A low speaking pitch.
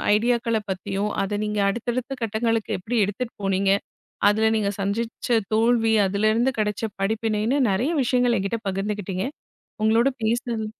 No: high, 220 Hz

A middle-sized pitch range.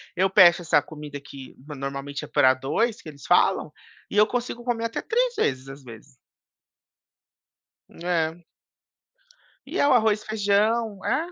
No: wide, 7.9 semitones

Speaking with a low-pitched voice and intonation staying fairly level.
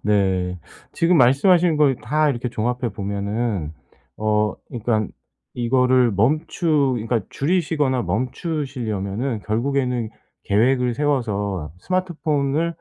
No: low, 125 Hz; wide, 5.4 semitones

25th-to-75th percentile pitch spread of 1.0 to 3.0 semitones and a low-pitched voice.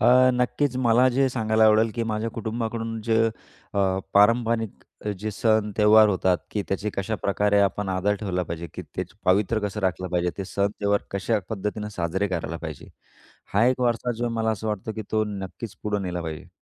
Yes: average, 2.7 semitones; low, 105 Hz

